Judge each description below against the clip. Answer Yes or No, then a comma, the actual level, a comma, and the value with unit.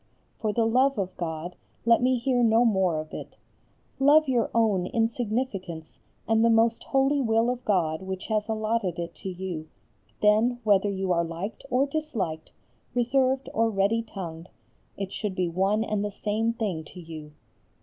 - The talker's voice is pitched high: Yes, high, 215 Hz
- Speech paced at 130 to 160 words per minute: No, average, 170 wpm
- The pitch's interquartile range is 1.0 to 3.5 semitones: No, average, 4.2 semitones